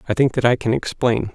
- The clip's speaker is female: No, male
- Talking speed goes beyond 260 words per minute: Yes, fast, 270 wpm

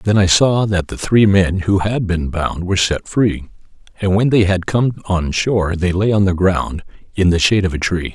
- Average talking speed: No, fast, 235 wpm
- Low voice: Yes, very low, 95 Hz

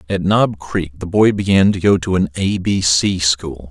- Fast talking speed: Yes, fast, 225 wpm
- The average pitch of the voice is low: Yes, very low, 90 Hz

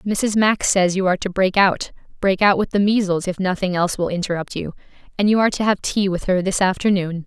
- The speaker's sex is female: Yes, female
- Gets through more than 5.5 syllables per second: Yes, 5.9 syllables/s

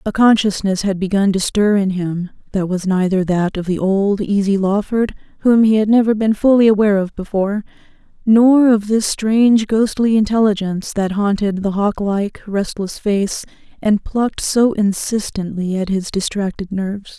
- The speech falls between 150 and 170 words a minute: Yes, average, 160 wpm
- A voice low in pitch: No, high, 205 Hz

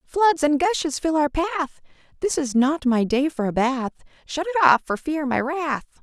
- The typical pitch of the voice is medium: No, very high, 295 Hz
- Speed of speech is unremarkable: No, fast, 210 wpm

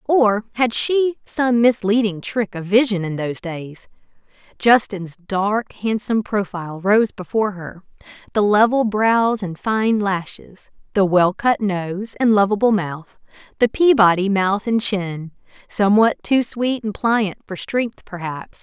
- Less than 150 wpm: Yes, average, 140 wpm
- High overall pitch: Yes, high, 205 Hz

